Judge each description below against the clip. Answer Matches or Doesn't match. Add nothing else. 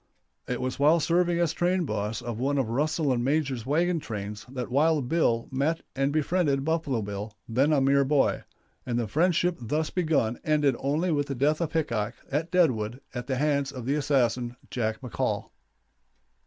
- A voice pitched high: Doesn't match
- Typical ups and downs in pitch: Matches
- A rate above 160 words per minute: Matches